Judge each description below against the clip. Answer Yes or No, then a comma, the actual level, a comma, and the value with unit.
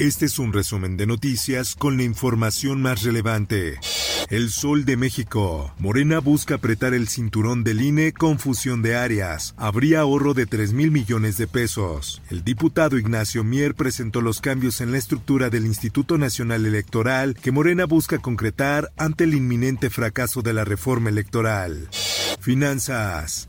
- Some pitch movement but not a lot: Yes, average, 4.1 semitones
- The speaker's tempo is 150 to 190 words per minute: Yes, average, 155 wpm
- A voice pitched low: Yes, low, 120 Hz